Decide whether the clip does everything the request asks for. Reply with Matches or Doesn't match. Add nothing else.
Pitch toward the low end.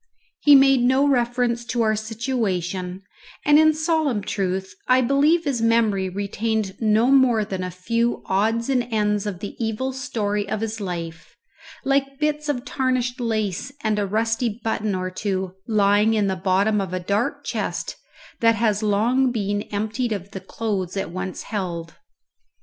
Doesn't match